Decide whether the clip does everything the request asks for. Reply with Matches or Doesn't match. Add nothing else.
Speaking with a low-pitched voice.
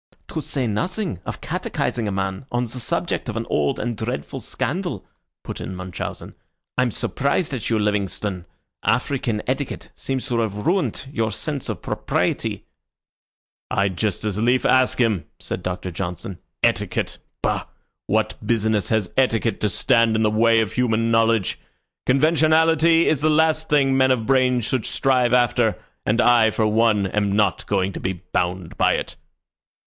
Matches